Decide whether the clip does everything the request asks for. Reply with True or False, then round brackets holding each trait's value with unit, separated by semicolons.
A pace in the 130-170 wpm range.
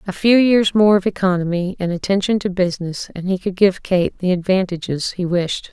False (200 wpm)